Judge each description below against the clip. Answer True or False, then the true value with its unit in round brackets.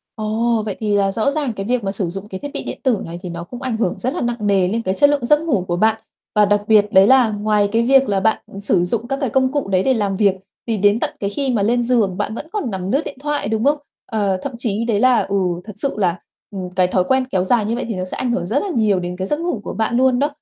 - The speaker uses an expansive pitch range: False (4.3 semitones)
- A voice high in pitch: True (220 Hz)